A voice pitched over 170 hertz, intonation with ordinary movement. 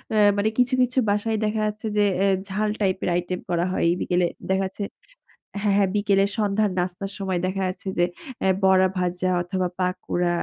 No: high, 190 Hz; narrow, 2.3 semitones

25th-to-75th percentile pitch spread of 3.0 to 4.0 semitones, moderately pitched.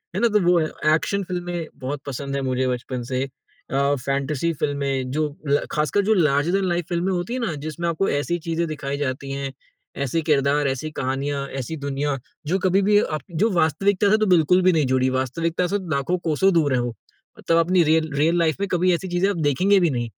No: average, 4.4 semitones; medium, 155 Hz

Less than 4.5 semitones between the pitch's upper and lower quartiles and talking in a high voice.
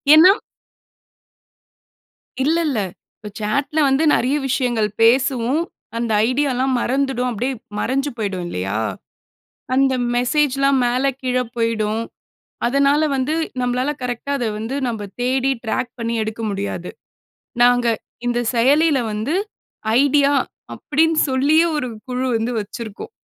Yes: average, 3.3 semitones; very high, 255 Hz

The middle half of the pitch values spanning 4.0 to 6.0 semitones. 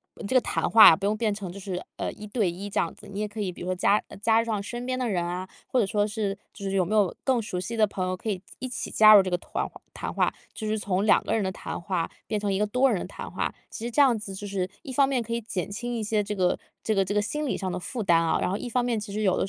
No: average, 3.2 semitones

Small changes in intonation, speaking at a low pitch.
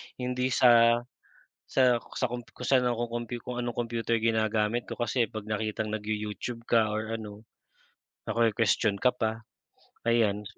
Yes: narrow, 1.8 semitones; low, 115 Hz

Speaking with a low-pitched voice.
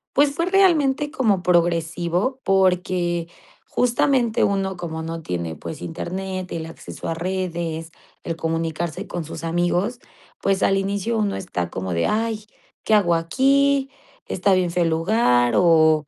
No: medium, 180 Hz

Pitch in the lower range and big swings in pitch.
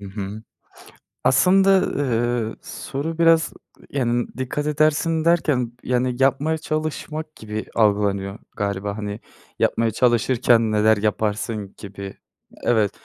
Yes: low, 120 Hz; wide, 6.1 semitones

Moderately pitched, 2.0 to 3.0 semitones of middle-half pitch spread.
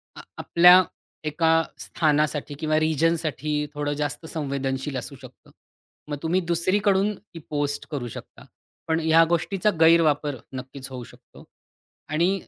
Yes: medium, 155 Hz; narrow, 2.6 semitones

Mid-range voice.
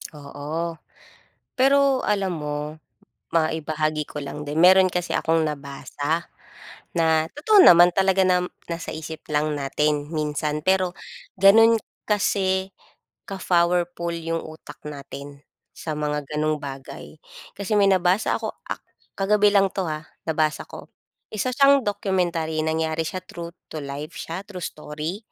Yes: medium, 165 Hz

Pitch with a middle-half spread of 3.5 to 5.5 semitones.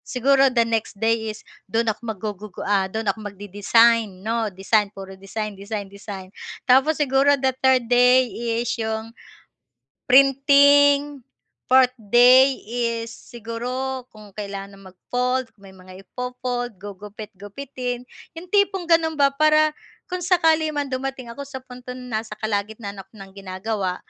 Yes: average, 4.4 semitones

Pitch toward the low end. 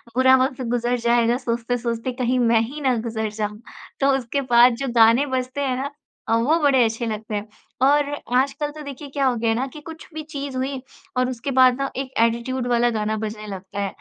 No: very high, 250 Hz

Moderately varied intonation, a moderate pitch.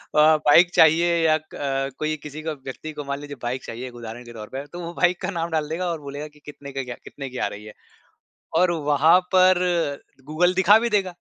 Yes: average, 4.0 semitones; medium, 150 Hz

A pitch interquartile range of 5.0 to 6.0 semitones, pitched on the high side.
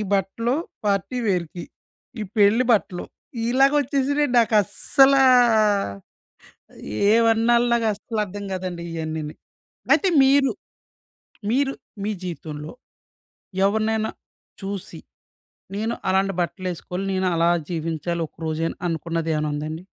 Yes: wide, 5.5 semitones; high, 195 Hz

